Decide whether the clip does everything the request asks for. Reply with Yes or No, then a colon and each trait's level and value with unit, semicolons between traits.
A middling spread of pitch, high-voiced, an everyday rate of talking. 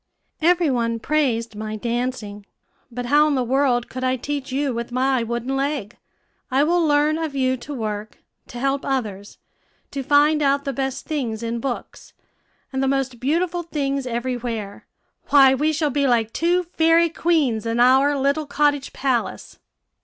Yes: average, 3.5 semitones; very high, 270 Hz; average, 170 wpm